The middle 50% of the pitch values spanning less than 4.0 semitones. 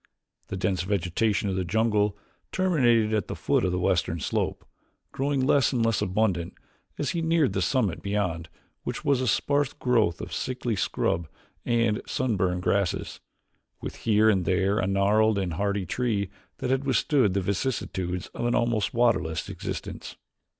No: average, 4.7 semitones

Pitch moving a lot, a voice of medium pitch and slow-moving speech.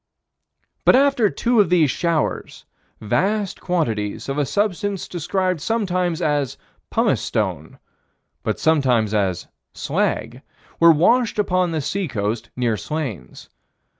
Yes: wide, 7.4 semitones; medium, 165 Hz; slow, 120 wpm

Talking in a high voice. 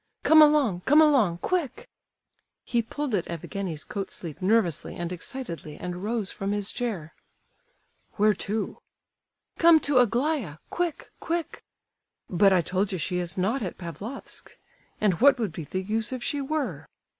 Yes: high, 210 Hz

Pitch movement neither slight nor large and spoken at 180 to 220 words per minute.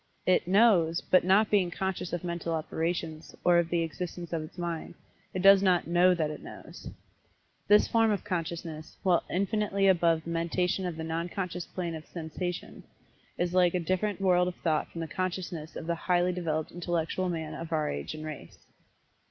No: narrow, 2.0 semitones; average, 185 wpm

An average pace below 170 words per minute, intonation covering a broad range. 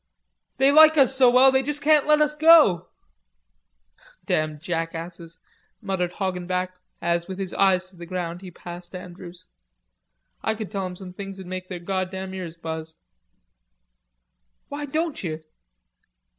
Yes: average, 145 wpm; wide, 6.5 semitones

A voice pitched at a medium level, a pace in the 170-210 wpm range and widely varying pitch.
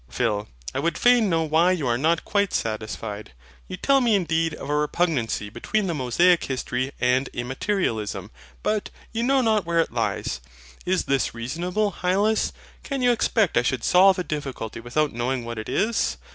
Yes: medium, 160 Hz; average, 175 wpm; wide, 8.2 semitones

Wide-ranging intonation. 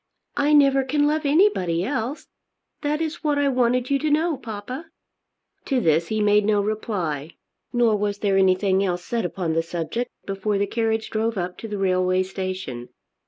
Yes: wide, 6.3 semitones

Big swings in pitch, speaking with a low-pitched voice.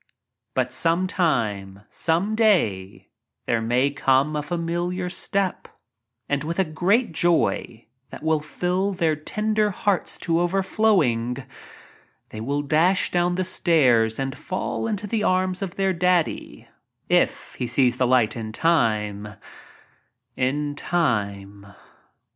No: wide, 7.0 semitones; medium, 160 Hz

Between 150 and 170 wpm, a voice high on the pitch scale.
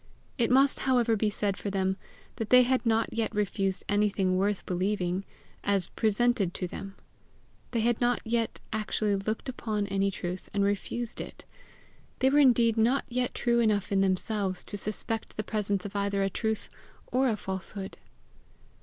Yes: average, 165 wpm; high, 210 Hz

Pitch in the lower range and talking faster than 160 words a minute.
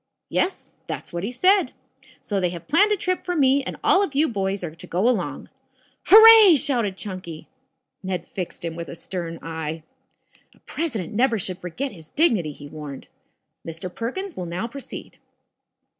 No: high, 200 Hz; average, 175 wpm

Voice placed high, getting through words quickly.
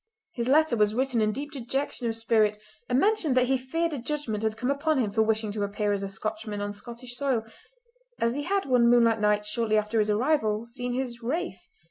Yes: high, 235 Hz; fast, 215 wpm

